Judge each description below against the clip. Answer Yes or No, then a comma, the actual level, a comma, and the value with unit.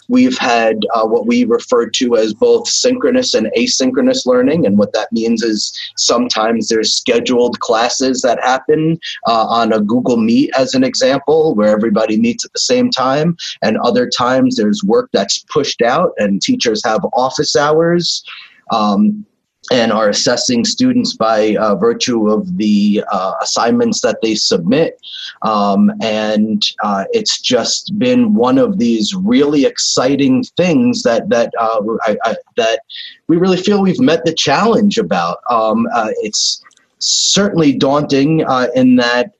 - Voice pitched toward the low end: No, medium, 180 Hz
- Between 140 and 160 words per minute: Yes, average, 155 wpm